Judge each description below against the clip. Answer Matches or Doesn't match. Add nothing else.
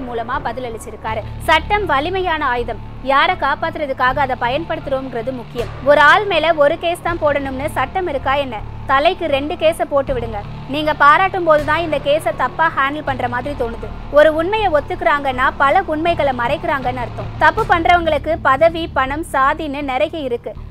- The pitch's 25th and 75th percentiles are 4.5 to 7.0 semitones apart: Doesn't match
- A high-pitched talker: Matches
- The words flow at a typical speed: Doesn't match